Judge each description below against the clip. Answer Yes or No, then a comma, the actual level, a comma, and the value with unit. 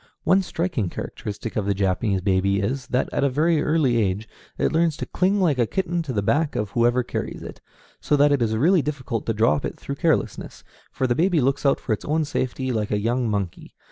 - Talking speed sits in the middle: No, fast, 225 wpm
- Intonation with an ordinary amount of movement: No, wide, 6.1 semitones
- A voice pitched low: Yes, low, 130 Hz